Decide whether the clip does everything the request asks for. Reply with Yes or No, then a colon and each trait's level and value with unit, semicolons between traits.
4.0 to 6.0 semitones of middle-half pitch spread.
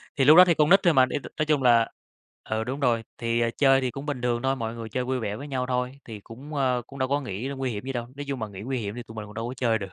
No: average, 3.0 semitones